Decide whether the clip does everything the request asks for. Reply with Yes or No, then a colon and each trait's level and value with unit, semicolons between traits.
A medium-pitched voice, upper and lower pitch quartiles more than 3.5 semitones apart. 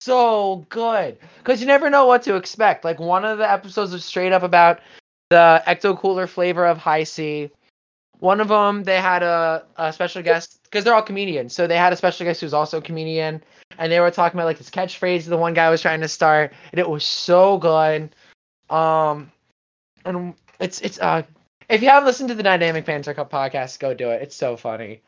No: medium, 170 Hz; average, 3.2 semitones